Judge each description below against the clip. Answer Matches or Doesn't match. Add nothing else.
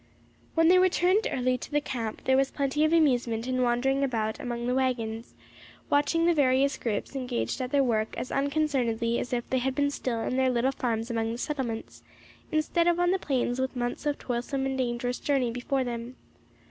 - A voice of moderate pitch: Doesn't match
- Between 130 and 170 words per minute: Doesn't match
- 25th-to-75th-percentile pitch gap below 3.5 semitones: Matches